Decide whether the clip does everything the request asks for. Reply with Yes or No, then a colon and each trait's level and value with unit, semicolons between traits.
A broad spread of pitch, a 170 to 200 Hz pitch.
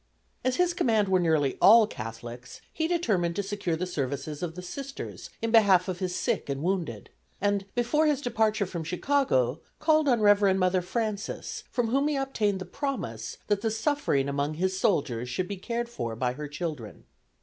Yes: wide, 7.5 semitones; high, 190 Hz